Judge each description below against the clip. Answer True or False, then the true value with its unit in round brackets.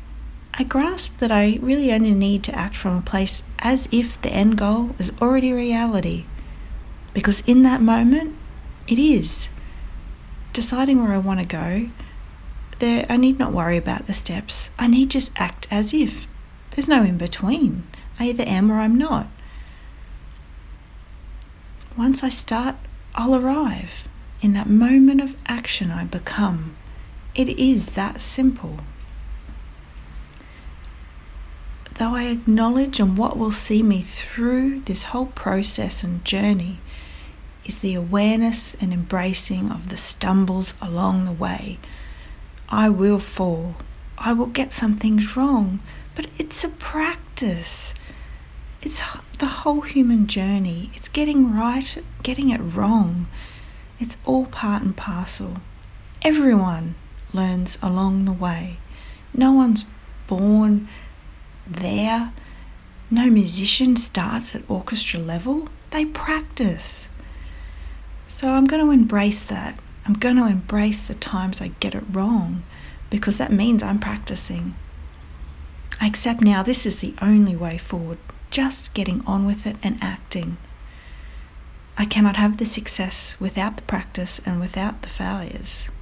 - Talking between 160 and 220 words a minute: False (135 wpm)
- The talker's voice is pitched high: True (205 Hz)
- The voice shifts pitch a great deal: True (6.0 semitones)